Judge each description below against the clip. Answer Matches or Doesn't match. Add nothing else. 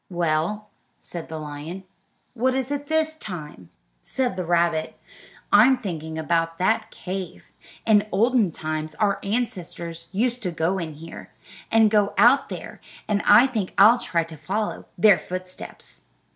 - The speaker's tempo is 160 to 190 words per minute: Doesn't match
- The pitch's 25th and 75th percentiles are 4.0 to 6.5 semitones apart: Matches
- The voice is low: Doesn't match